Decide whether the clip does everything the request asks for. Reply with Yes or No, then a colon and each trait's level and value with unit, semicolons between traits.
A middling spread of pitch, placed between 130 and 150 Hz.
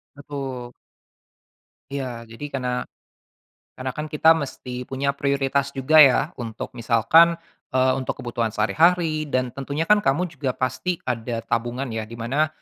Yes: average, 3.2 semitones; low, 135 Hz